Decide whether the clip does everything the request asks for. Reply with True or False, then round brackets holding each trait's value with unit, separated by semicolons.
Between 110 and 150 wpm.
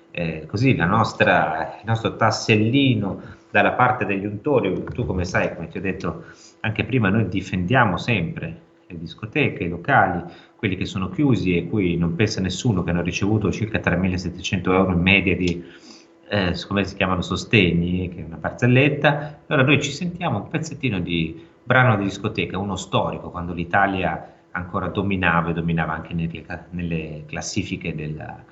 False (160 wpm)